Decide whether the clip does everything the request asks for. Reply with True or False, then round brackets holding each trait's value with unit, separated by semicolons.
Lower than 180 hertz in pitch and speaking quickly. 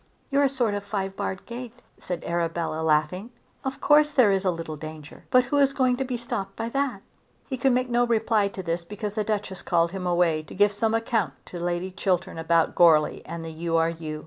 False (195 Hz; 225 wpm)